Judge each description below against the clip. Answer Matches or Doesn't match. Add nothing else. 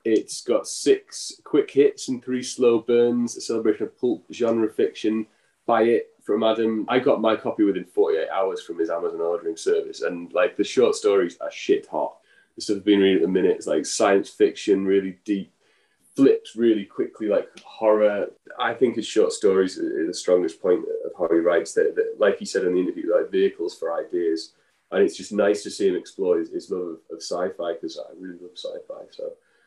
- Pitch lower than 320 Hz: Doesn't match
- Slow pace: Doesn't match